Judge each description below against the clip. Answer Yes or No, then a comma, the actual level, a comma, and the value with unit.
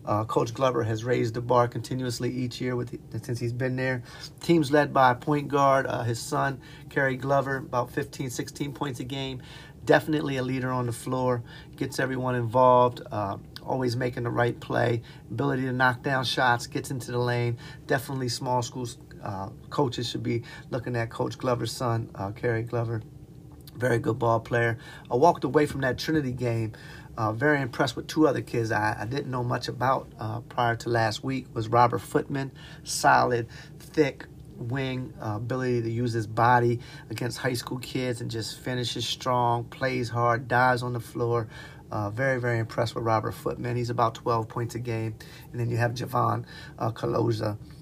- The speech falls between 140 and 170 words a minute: No, average, 185 wpm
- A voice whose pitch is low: Yes, low, 125 Hz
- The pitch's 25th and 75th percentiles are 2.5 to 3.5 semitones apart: Yes, average, 3.1 semitones